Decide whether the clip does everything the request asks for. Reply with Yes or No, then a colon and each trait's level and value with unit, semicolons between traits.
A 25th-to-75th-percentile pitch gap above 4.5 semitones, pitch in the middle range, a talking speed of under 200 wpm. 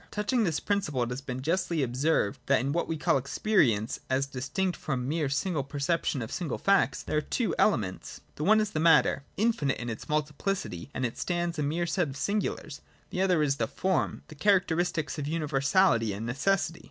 No: average, 5.2 semitones; medium, 155 Hz; fast, 205 wpm